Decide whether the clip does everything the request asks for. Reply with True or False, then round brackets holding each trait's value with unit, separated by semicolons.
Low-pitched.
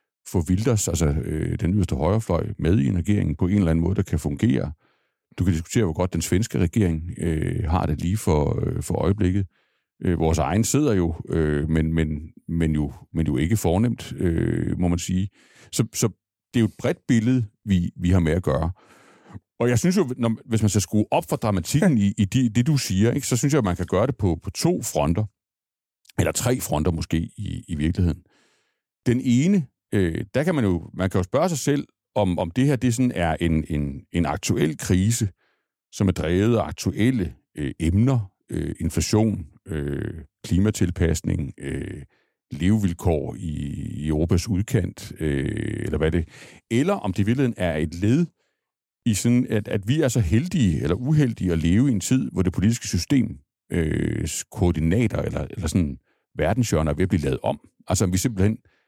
True (95 Hz)